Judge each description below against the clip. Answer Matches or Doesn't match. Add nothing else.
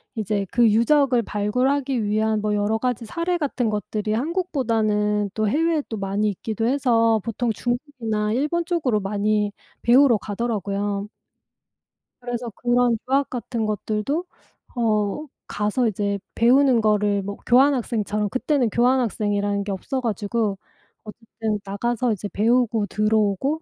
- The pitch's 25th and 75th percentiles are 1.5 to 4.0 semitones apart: Matches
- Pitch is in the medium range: Doesn't match